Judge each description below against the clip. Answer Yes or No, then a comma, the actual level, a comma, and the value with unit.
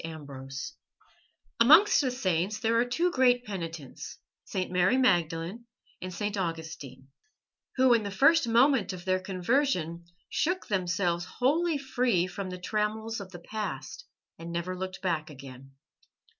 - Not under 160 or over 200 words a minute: No, average, 140 wpm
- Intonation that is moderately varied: No, wide, 6.3 semitones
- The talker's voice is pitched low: No, high, 190 Hz